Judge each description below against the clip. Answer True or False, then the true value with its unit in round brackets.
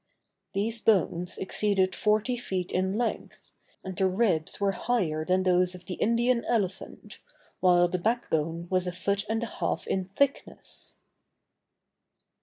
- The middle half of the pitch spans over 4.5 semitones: False (3.5 semitones)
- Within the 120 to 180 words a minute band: True (145 wpm)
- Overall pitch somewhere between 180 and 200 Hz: True (190 Hz)